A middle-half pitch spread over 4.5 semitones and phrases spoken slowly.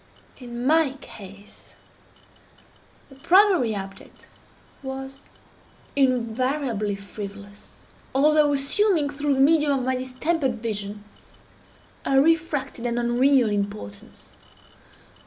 Yes: average, 4.9 semitones; slow, 90 wpm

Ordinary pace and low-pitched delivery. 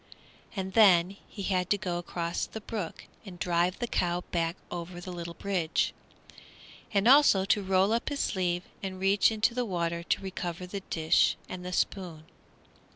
No: average, 170 wpm; medium, 185 Hz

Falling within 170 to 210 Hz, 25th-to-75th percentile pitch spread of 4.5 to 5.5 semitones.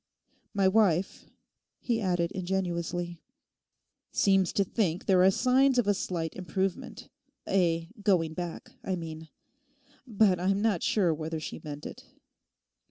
No: medium, 185 Hz; average, 2.8 semitones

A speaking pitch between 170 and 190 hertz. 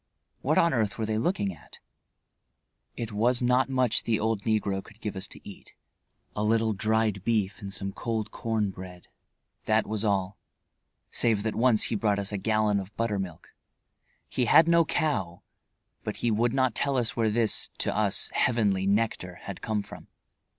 No: low, 110 Hz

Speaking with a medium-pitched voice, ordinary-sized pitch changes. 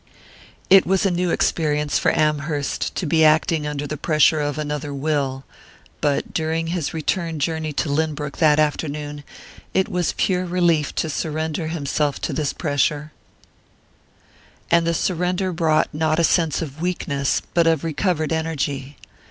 No: medium, 155 Hz; narrow, 2.2 semitones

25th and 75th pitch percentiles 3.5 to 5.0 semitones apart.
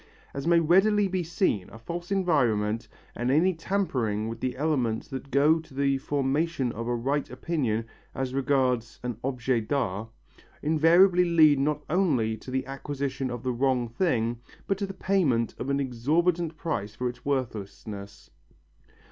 No: wide, 5.6 semitones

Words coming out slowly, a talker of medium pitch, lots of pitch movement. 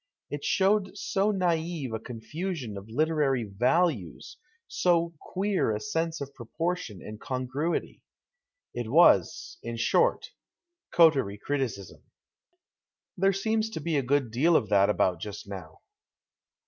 Yes: slow, 130 wpm; medium, 145 Hz; wide, 7.6 semitones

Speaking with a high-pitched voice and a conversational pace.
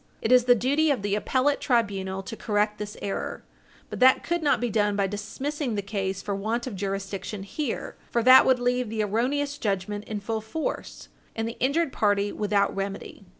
Yes: high, 215 Hz; average, 195 wpm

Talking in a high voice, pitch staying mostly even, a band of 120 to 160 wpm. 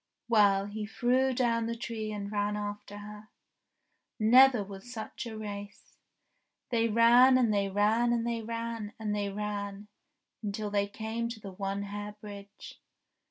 Yes: high, 210 Hz; narrow, 2.2 semitones; average, 155 wpm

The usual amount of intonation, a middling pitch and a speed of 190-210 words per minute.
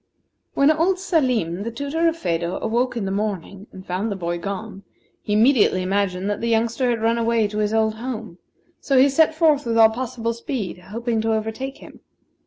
No: average, 4.1 semitones; high, 225 Hz; average, 195 wpm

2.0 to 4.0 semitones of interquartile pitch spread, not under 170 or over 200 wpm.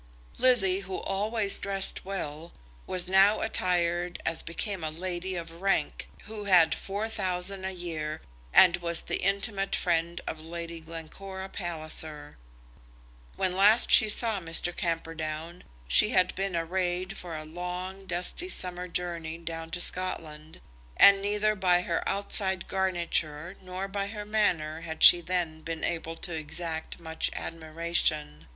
No: average, 2.8 semitones; average, 140 wpm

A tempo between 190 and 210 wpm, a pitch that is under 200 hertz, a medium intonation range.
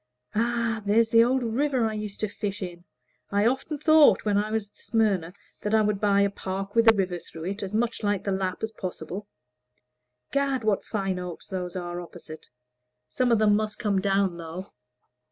No: average, 195 wpm; high, 205 Hz; average, 3.0 semitones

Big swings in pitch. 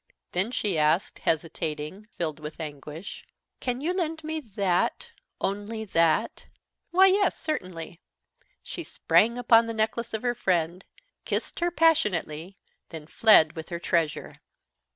Yes: wide, 6.7 semitones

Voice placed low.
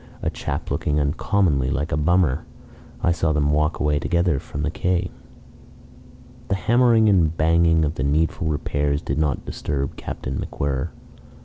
Yes: very low, 75 Hz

